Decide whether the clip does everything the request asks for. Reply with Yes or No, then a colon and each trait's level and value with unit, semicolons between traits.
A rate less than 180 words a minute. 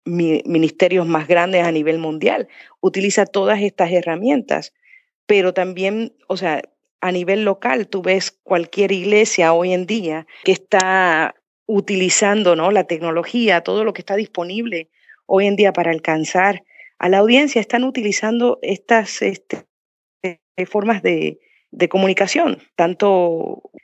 Yes: average, 130 wpm